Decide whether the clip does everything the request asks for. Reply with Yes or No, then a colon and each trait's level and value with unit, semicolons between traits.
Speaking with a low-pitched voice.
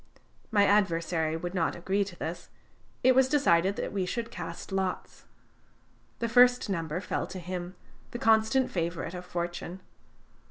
No: medium, 185 Hz